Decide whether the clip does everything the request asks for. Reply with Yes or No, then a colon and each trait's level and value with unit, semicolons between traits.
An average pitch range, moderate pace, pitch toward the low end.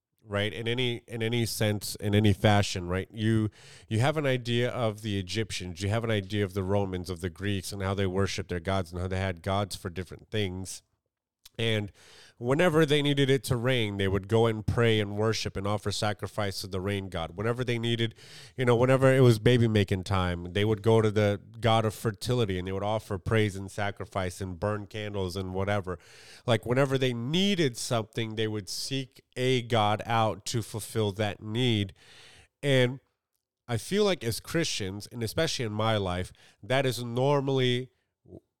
Yes: average, 3.4 semitones; average, 190 wpm; low, 110 Hz